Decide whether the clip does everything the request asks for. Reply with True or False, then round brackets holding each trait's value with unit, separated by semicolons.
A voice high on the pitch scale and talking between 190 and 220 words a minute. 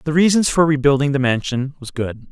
False (140 Hz; 205 wpm)